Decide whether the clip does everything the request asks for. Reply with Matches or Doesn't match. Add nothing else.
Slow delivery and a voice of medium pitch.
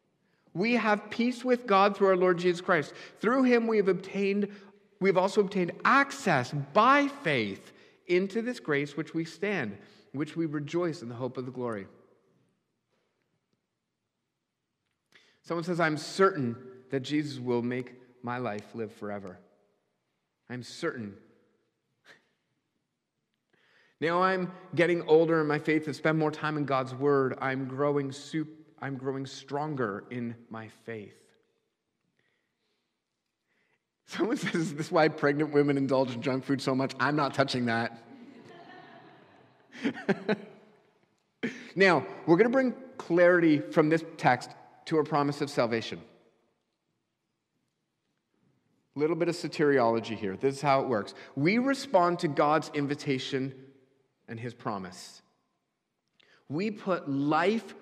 Matches